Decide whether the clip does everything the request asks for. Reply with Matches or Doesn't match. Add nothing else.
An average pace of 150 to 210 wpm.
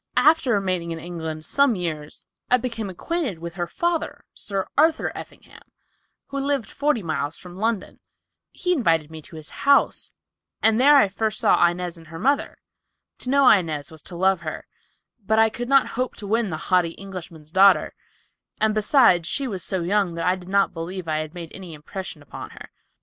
Matches